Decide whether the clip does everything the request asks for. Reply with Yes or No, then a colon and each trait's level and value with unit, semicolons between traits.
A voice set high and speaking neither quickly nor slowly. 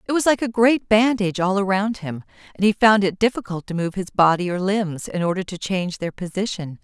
No: high, 195 Hz; fast, 230 wpm